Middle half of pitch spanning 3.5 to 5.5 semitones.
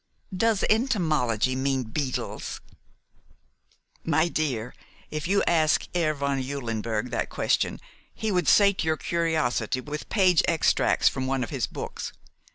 Yes: average, 5.0 semitones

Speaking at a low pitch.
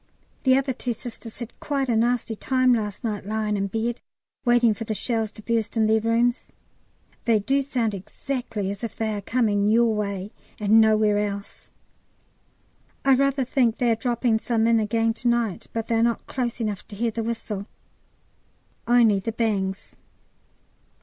No: high, 225 Hz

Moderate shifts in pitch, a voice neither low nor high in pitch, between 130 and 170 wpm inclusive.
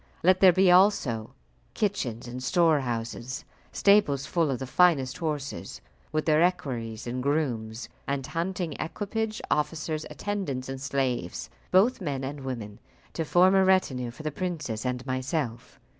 No: wide, 5.9 semitones; medium, 145 Hz; average, 145 wpm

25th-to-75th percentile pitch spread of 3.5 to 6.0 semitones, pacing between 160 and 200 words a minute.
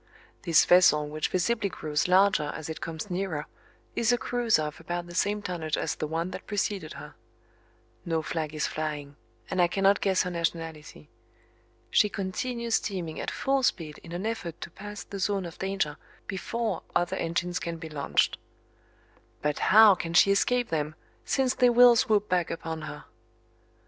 Yes: average, 4.3 semitones; average, 170 wpm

